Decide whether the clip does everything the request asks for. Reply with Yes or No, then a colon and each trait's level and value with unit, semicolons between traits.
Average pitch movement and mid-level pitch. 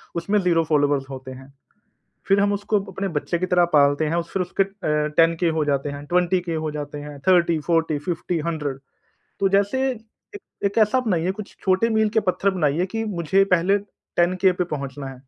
Yes: average, 4.6 semitones; medium, 170 Hz